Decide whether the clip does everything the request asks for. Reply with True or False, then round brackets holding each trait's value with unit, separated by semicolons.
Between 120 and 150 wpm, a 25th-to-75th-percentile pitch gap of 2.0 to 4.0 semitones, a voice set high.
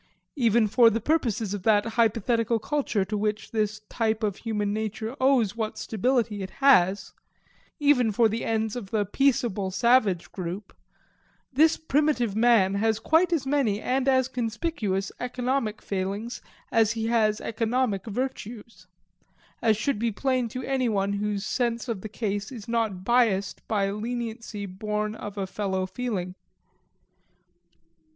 True (145 wpm; 3.0 semitones; 220 Hz)